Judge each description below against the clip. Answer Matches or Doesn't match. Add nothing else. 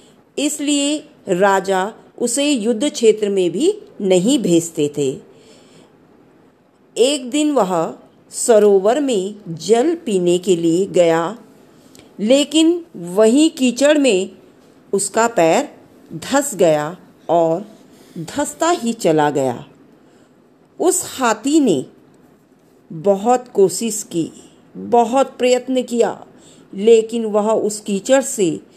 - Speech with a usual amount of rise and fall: Doesn't match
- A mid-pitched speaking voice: Doesn't match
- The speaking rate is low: Matches